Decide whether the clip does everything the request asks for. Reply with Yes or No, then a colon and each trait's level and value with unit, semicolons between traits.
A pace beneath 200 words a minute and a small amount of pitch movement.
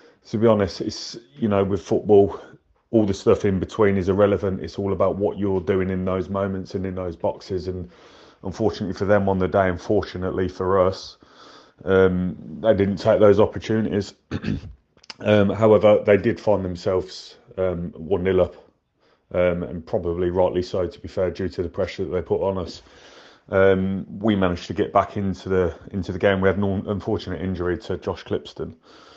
Yes: average, 185 wpm; narrow, 1.8 semitones